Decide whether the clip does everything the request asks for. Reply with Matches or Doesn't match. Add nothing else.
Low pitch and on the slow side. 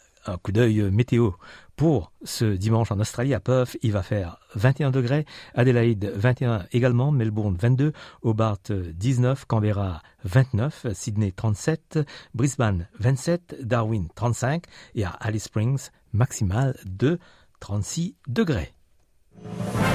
Matches